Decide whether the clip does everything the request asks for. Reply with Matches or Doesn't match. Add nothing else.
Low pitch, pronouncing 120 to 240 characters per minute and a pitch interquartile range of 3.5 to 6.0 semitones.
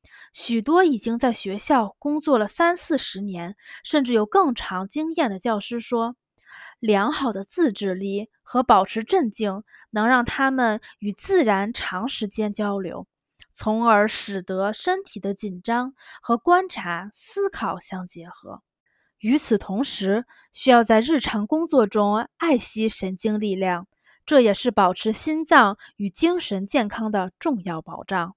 Doesn't match